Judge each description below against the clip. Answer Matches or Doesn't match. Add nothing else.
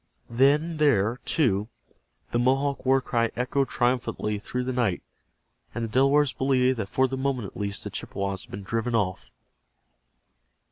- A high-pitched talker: Doesn't match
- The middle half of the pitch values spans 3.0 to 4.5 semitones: Matches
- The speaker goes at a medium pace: Matches